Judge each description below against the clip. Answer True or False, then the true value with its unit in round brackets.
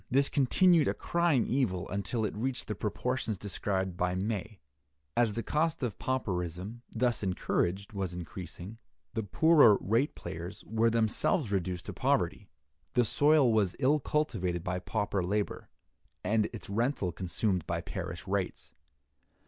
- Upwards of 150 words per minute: False (140 wpm)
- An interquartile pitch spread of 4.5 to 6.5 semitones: True (5.1 semitones)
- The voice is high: False (105 Hz)